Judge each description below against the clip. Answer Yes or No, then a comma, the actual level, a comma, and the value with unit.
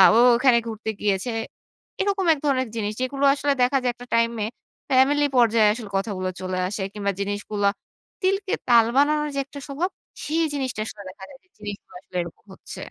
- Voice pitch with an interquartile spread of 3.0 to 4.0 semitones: No, wide, 5.5 semitones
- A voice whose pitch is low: No, high, 240 Hz